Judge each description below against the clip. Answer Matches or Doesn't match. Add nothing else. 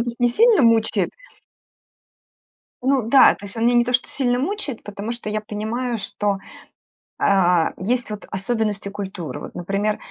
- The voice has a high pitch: Matches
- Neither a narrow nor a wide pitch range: Matches